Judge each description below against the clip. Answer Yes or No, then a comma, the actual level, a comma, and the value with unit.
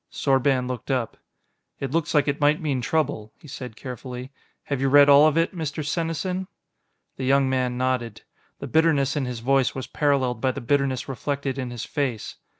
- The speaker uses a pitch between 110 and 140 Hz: Yes, low, 135 Hz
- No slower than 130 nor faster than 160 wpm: No, average, 185 wpm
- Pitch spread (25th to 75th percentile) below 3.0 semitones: Yes, narrow, 2.5 semitones